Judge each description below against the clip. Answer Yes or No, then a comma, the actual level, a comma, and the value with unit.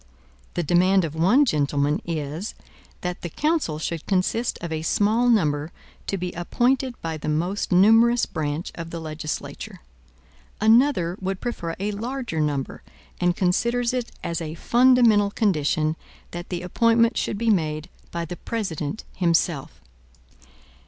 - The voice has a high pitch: No, medium, 180 Hz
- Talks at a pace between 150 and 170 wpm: No, average, 140 wpm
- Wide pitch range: Yes, wide, 6.2 semitones